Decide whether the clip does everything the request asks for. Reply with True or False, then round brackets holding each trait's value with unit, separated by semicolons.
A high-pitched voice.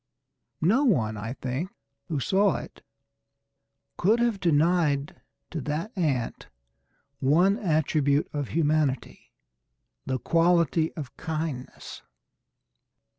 False (155 Hz)